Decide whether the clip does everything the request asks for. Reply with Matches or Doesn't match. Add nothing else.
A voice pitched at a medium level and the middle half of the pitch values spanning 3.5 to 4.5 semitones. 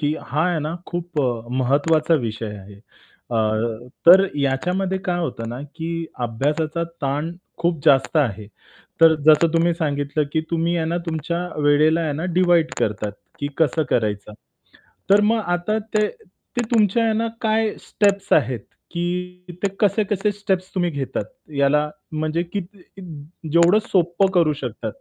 Matches